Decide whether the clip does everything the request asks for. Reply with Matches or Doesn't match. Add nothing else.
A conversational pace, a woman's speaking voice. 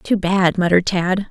Matches